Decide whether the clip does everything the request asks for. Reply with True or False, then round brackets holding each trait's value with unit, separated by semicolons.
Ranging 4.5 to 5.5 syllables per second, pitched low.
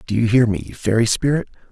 False (6.6 syllables/s; 110 Hz)